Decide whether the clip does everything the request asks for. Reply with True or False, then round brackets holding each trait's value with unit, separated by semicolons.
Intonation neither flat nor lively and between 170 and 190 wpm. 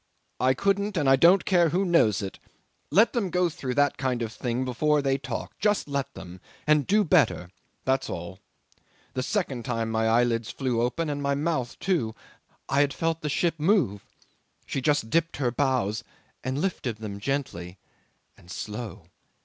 False (6.0 semitones; 175 wpm)